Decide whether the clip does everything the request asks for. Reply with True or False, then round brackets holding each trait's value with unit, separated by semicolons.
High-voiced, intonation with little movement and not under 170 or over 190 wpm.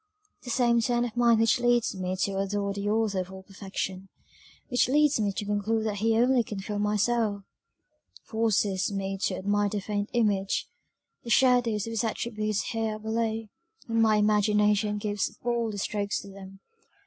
True (210 Hz; 2.2 semitones; 175 wpm)